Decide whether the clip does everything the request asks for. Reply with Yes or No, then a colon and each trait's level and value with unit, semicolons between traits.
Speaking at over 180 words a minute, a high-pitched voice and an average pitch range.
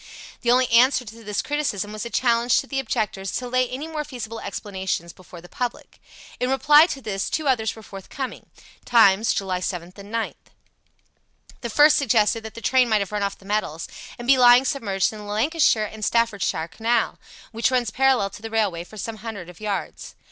Yes: average, 200 wpm; high, 225 Hz; average, 3.9 semitones